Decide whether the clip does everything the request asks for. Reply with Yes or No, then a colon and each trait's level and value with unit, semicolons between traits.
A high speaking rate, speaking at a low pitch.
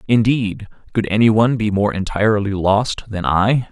No: average, 145 wpm; low, 105 Hz